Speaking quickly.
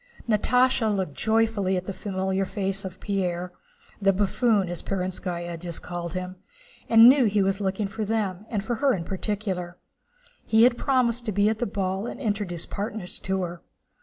No: average, 175 wpm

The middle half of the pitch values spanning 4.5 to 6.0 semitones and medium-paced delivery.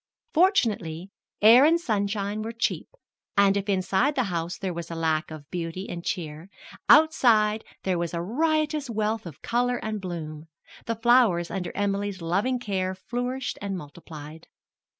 Yes: wide, 5.6 semitones; average, 150 wpm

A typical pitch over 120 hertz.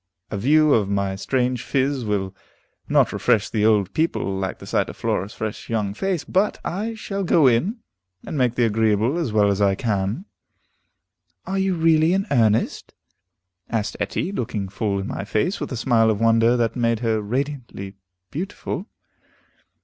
No: low, 115 Hz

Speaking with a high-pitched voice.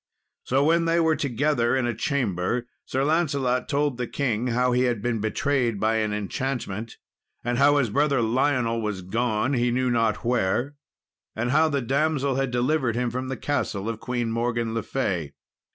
No: low, 125 Hz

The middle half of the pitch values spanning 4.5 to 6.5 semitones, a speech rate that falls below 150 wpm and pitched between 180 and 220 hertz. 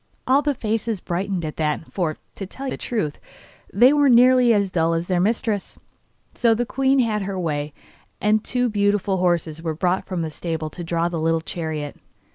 No: wide, 5.6 semitones; average, 190 wpm; high, 190 Hz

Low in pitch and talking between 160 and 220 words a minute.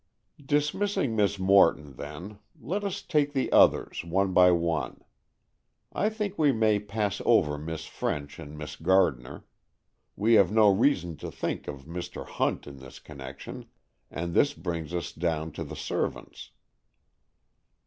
No: very low, 90 Hz; average, 145 wpm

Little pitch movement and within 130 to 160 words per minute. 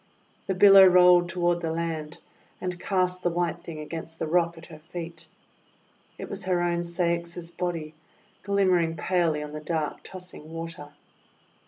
Yes: narrow, 1.6 semitones; average, 155 wpm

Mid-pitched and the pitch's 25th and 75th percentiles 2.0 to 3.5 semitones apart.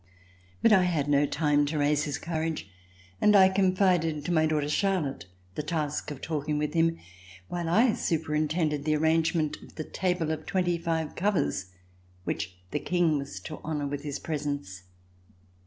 Yes: medium, 155 Hz; average, 2.7 semitones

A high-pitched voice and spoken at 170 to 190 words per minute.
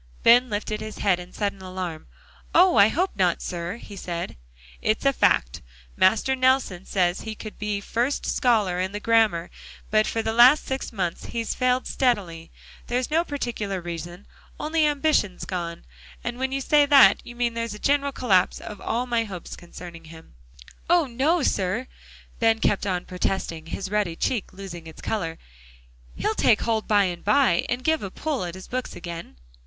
Yes: high, 210 Hz; average, 180 wpm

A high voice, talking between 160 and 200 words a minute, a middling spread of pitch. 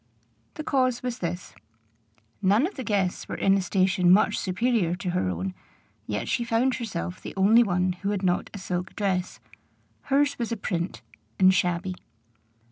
Yes: high, 195 Hz; average, 170 wpm; average, 4.5 semitones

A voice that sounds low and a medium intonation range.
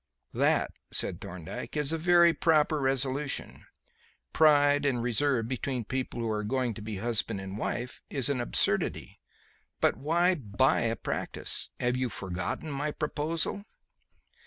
Yes: low, 130 Hz; average, 4.5 semitones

